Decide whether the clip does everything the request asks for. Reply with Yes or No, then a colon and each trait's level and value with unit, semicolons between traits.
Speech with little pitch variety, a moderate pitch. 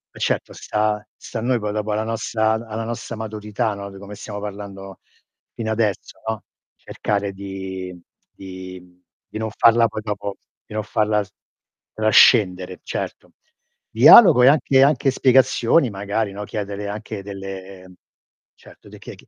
No: narrow, 2.2 semitones; low, 105 Hz